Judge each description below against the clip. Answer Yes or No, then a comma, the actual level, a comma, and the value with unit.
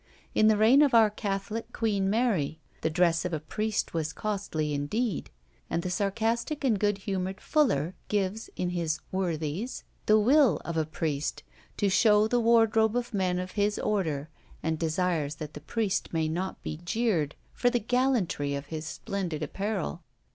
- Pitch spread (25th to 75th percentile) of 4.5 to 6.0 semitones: Yes, wide, 5.5 semitones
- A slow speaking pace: No, average, 170 wpm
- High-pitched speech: Yes, high, 195 Hz